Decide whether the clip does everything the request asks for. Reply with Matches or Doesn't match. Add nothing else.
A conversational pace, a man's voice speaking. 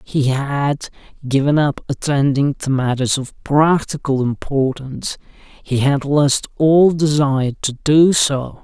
Doesn't match